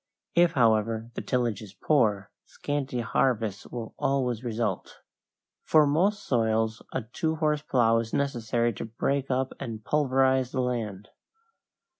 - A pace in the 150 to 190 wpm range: No, slow, 135 wpm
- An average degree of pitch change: Yes, average, 3.6 semitones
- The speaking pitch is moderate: No, low, 120 Hz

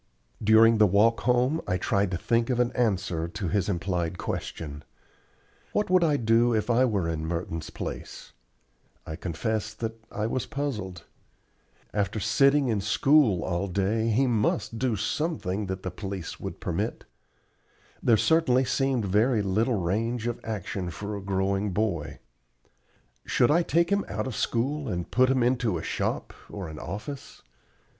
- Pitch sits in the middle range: No, low, 110 Hz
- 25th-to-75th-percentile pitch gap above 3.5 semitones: Yes, average, 4.6 semitones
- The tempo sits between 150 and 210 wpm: Yes, average, 160 wpm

